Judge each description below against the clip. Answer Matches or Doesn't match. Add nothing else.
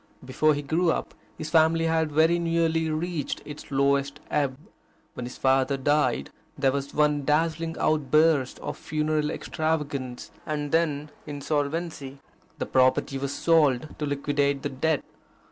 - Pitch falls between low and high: Matches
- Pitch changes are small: Matches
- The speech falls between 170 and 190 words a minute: Doesn't match